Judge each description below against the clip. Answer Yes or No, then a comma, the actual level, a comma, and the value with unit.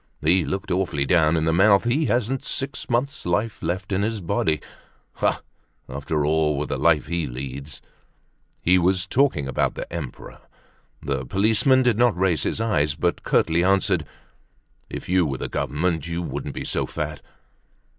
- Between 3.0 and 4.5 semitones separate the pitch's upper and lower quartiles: No, average, 5.2 semitones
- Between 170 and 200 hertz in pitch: No, very low, 85 Hz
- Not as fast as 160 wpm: No, average, 165 wpm